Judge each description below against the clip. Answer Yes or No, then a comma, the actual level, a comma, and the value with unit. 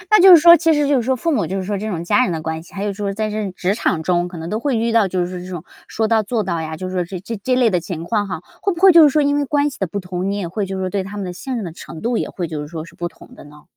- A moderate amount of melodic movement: No, wide, 5.8 semitones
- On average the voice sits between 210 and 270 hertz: No, high, 200 Hz